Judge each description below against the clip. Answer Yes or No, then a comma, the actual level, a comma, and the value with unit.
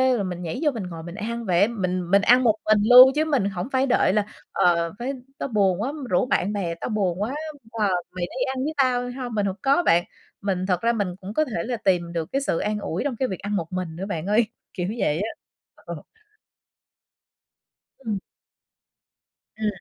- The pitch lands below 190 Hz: No, high, 205 Hz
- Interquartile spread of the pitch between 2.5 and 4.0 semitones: No, average, 5.1 semitones